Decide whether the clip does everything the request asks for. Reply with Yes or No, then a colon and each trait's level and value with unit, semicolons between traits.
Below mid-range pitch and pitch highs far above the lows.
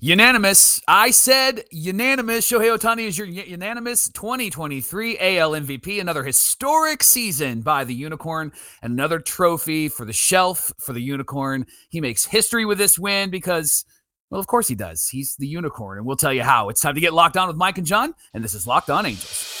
No: medium, 175 Hz; wide, 7.7 semitones